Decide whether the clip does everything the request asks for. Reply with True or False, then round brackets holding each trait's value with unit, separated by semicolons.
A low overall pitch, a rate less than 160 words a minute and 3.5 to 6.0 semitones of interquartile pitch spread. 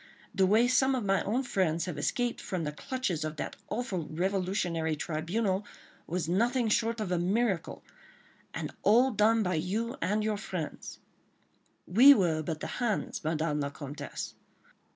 False (190 Hz; 150 wpm; 5.6 semitones)